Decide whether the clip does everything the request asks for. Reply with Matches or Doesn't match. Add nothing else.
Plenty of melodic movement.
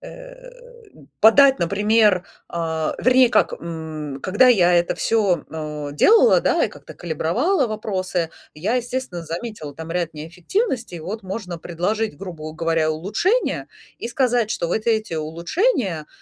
Matches